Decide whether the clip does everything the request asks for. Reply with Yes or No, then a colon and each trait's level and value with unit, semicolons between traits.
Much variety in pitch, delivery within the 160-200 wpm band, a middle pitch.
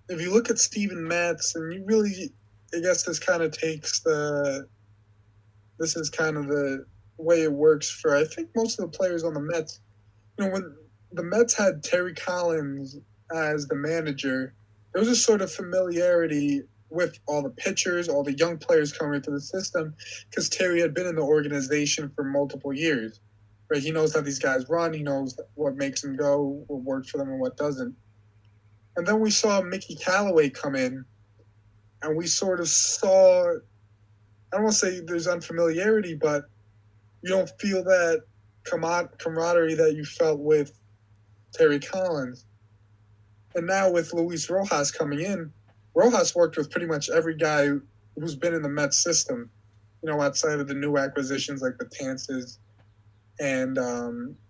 Yes: wide, 5.9 semitones; average, 175 wpm; medium, 150 Hz